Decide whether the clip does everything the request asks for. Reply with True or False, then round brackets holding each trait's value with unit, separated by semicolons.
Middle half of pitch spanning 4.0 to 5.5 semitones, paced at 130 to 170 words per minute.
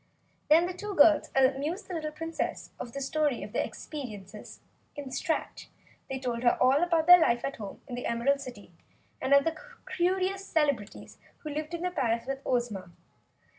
False (5.1 semitones; 185 wpm)